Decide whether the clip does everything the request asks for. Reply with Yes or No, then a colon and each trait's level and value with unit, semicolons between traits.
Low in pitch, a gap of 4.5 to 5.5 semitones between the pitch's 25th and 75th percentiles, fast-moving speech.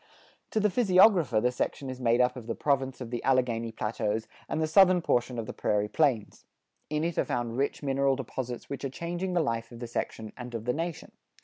Yes: low, 130 Hz; average, 5.1 semitones; fast, 220 wpm